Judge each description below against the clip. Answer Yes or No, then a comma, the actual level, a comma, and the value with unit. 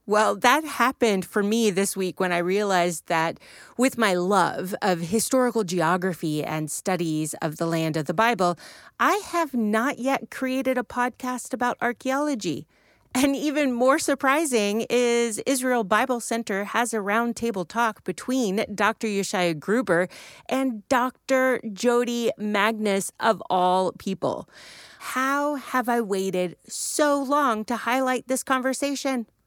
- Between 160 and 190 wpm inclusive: No, slow, 135 wpm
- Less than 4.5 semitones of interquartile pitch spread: No, average, 5.1 semitones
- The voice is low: No, high, 230 Hz